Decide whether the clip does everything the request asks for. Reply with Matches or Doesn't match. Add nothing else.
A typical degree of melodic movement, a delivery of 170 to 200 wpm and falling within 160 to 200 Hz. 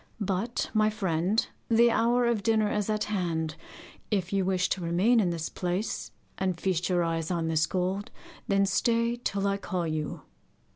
Matches